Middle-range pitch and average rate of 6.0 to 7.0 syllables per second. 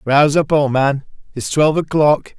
No: medium, 145 Hz; 5.0 syllables/s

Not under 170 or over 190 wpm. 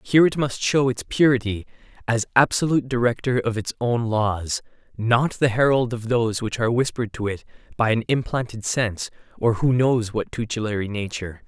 Yes: average, 175 wpm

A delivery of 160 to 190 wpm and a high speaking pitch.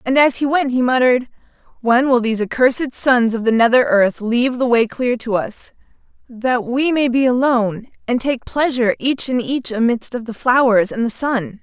No: average, 200 wpm; high, 245 Hz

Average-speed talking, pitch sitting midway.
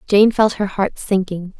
No: average, 190 wpm; high, 200 Hz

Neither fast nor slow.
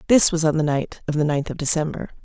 No: fast, 270 wpm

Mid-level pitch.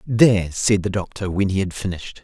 No: low, 100 Hz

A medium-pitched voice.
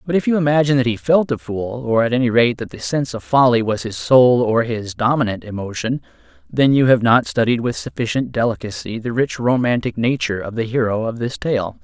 No: low, 120 Hz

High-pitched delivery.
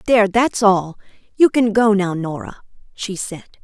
Yes: high, 205 Hz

